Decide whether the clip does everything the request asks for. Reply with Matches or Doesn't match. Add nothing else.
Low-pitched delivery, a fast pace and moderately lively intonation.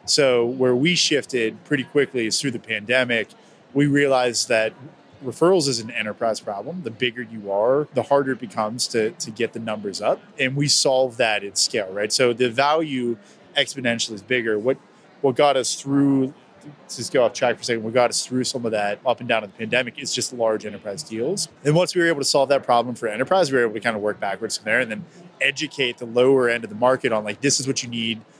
Matches